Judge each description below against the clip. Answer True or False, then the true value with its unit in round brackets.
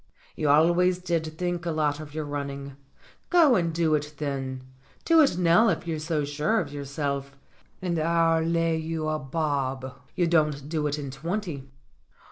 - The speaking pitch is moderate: True (155 Hz)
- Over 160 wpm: True (175 wpm)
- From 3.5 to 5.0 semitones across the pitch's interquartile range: False (3.0 semitones)